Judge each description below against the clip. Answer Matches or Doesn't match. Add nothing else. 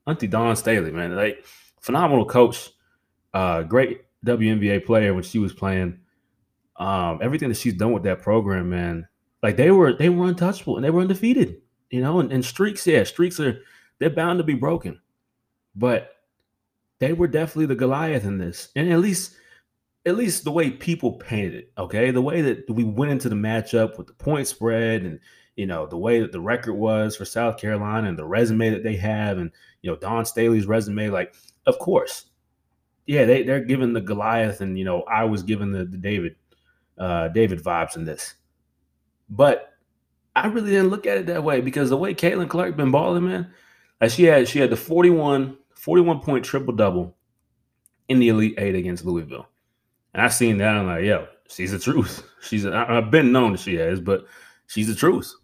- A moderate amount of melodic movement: Doesn't match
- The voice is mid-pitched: Doesn't match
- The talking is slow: Doesn't match